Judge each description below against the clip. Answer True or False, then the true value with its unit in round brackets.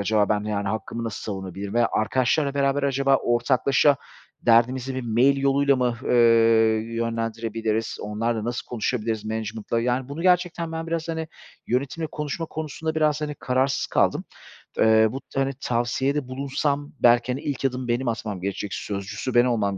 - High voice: False (125 Hz)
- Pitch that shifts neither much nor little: True (3.9 semitones)